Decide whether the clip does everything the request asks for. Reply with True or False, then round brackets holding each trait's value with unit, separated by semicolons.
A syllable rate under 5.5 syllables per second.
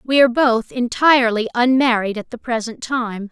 True (5.1 syllables/s)